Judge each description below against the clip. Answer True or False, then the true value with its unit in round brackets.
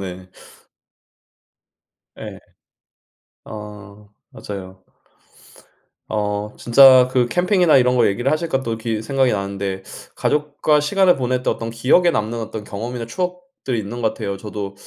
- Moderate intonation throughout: True (4.7 semitones)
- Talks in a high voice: False (115 Hz)